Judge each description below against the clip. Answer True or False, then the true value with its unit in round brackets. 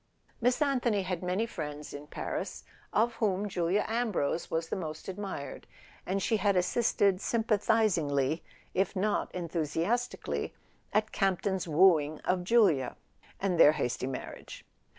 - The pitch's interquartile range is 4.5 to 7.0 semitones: True (4.9 semitones)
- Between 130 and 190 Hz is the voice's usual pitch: True (185 Hz)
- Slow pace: True (130 wpm)